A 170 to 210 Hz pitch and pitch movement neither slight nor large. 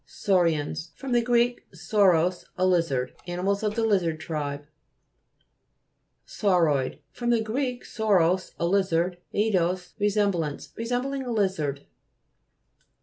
Yes: medium, 185 Hz; average, 4.6 semitones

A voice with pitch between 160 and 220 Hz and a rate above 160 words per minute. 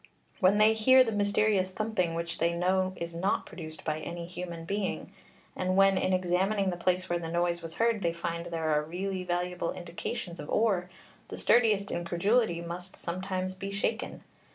Yes: medium, 185 Hz; average, 175 wpm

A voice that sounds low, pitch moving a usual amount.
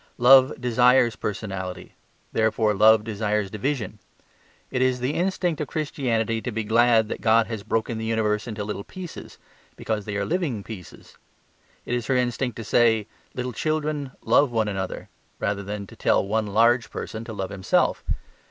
Yes: low, 115 Hz; average, 3.0 semitones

